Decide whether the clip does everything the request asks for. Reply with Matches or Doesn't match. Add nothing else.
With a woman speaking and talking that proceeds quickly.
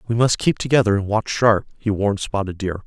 Doesn't match